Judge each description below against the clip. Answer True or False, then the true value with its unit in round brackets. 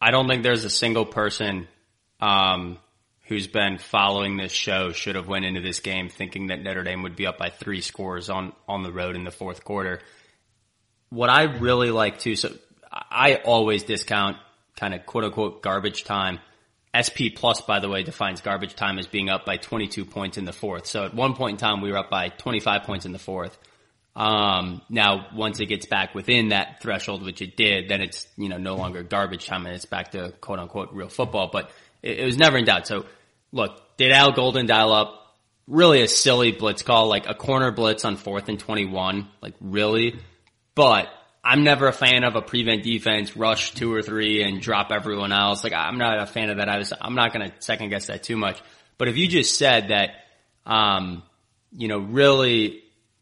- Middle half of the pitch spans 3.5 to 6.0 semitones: False (2.8 semitones)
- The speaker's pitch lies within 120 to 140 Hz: False (105 Hz)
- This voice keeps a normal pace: False (210 wpm)